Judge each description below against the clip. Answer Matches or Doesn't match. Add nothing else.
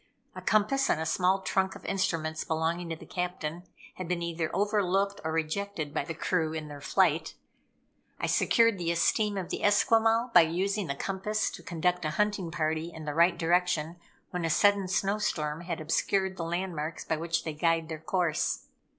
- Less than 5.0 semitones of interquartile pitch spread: Matches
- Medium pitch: Matches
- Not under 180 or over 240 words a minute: Matches